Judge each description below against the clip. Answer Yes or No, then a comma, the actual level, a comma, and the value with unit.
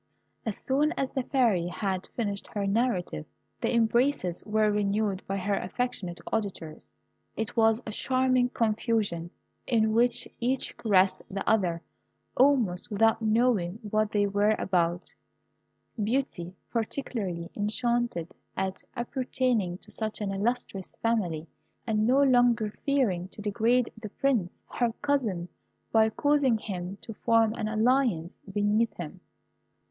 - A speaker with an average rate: No, slow, 130 wpm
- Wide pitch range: No, average, 3.8 semitones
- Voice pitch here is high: Yes, high, 215 Hz